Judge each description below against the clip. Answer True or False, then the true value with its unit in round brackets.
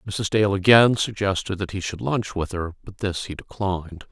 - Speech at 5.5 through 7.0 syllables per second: False (5.0 syllables/s)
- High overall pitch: False (100 Hz)